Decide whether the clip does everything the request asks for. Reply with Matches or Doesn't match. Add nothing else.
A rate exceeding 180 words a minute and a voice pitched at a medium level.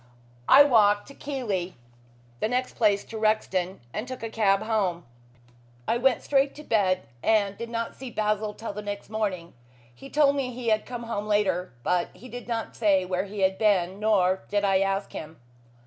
Doesn't match